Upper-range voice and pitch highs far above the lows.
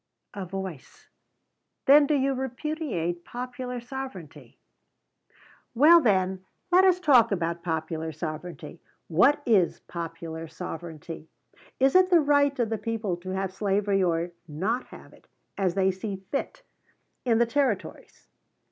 Yes: high, 195 Hz; wide, 7.5 semitones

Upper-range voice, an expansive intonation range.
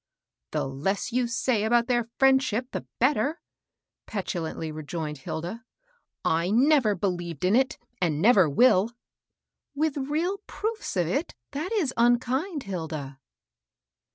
Yes: high, 230 Hz; wide, 7.5 semitones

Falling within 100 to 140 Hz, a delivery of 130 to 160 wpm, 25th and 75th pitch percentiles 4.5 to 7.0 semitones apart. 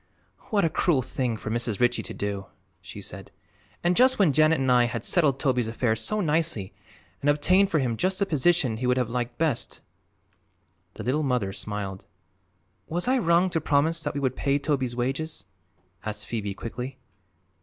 No: low, 135 Hz; average, 180 wpm; wide, 5.6 semitones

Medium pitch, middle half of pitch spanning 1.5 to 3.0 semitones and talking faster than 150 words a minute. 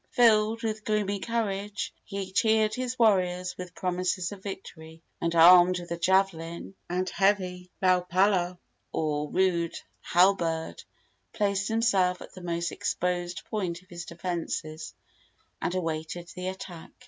No: medium, 180 Hz; narrow, 2.5 semitones; slow, 135 wpm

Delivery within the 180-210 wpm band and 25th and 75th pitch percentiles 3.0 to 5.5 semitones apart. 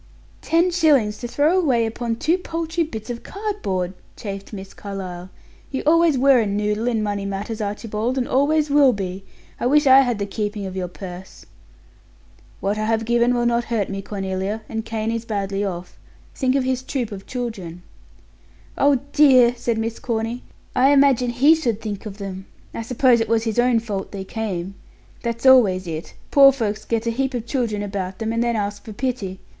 Yes: average, 190 wpm; average, 4.1 semitones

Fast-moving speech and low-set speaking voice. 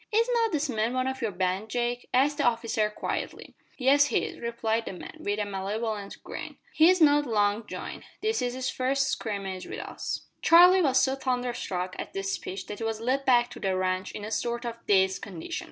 No: fast, 210 wpm; high, 235 Hz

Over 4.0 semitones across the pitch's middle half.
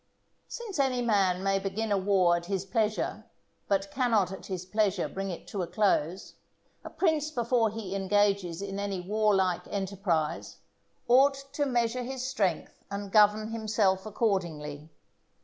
No: average, 3.1 semitones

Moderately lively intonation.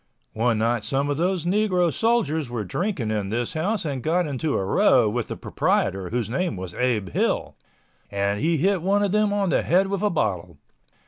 No: wide, 9.0 semitones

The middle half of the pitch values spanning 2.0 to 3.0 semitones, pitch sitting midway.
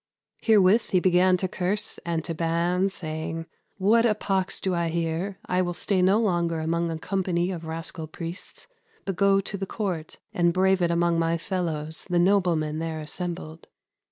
Yes: narrow, 2.5 semitones; medium, 175 Hz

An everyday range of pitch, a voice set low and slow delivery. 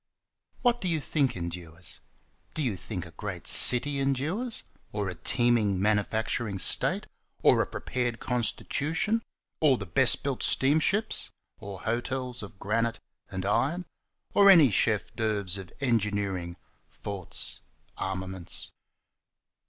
No: wide, 6.1 semitones; low, 110 Hz; slow, 120 wpm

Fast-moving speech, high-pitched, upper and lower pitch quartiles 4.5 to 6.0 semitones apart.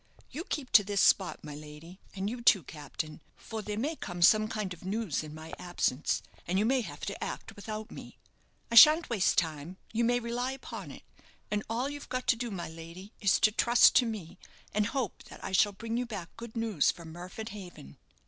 Yes: fast, 215 wpm; high, 205 Hz; average, 5.1 semitones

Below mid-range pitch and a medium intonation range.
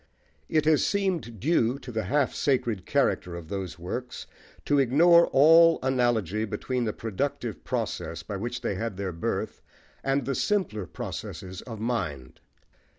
No: low, 120 Hz; wide, 6.1 semitones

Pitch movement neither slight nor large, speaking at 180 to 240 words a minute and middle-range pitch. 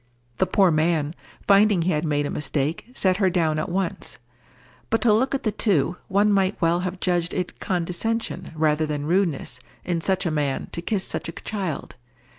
Yes: average, 4.0 semitones; average, 190 wpm; medium, 175 Hz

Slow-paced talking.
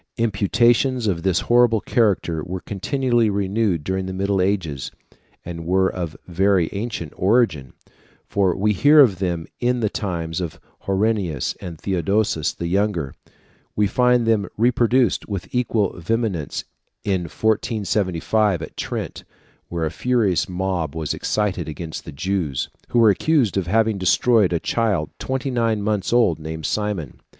No: average, 145 wpm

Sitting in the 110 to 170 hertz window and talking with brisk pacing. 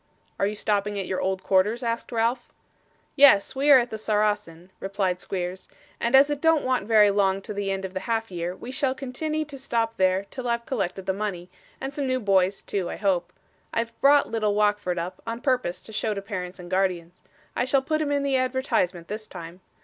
No: high, 210 Hz; fast, 215 wpm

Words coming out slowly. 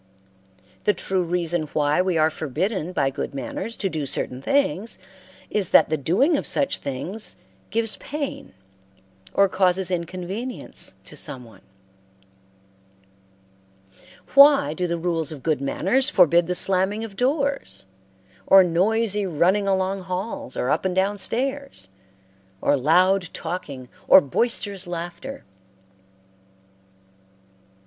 Yes: slow, 125 wpm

